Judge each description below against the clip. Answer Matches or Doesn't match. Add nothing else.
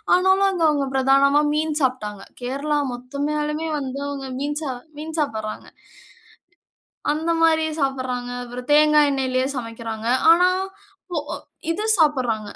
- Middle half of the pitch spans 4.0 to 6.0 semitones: Doesn't match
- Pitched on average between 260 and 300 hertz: Matches